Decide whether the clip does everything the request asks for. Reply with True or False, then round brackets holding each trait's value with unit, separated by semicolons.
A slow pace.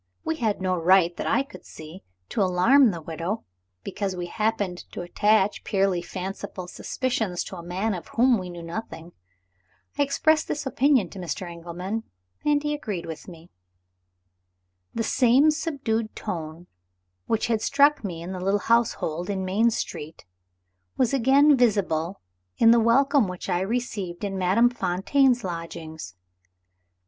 False (150 wpm)